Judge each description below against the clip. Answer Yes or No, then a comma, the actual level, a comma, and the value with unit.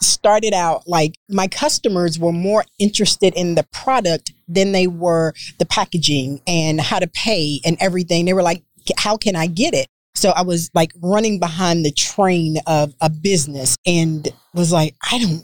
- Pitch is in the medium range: Yes, medium, 175 Hz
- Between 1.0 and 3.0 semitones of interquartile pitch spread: No, average, 3.4 semitones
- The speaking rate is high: No, average, 180 wpm